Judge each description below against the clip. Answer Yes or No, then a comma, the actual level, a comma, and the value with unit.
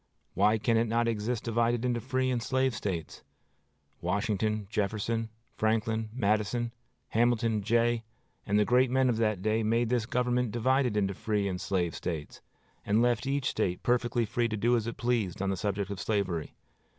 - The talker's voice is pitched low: Yes, low, 115 Hz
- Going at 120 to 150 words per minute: No, average, 175 wpm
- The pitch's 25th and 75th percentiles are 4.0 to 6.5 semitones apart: No, narrow, 2.6 semitones